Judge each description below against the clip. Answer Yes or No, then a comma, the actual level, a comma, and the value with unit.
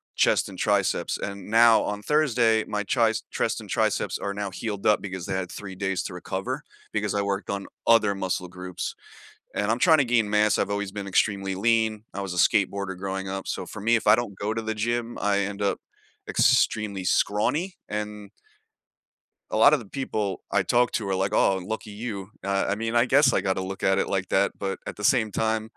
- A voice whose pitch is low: Yes, low, 105 Hz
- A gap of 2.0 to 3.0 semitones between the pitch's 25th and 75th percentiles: Yes, narrow, 2.4 semitones